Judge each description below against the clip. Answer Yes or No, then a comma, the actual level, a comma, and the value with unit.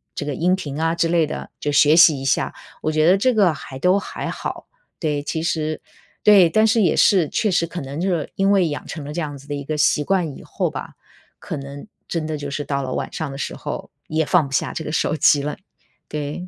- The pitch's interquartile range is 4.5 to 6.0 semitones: No, average, 3.4 semitones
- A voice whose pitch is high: No, medium, 155 Hz